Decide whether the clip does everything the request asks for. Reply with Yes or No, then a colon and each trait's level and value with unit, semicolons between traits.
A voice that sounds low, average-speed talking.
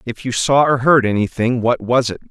No: low, 120 Hz; fast, 235 wpm